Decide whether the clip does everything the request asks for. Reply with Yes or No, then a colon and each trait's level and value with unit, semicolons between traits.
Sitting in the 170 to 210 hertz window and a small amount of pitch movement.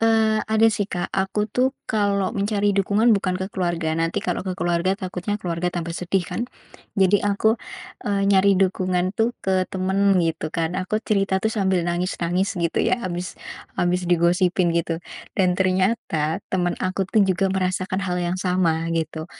Yes: medium, 185 Hz; narrow, 2.2 semitones